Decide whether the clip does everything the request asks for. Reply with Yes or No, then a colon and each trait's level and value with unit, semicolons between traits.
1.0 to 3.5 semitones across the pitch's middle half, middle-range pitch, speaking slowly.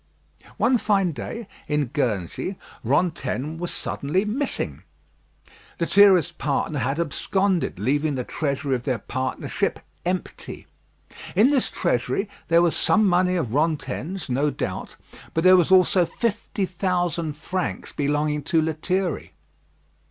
No: average, 4.6 semitones; medium, 165 Hz; slow, 120 wpm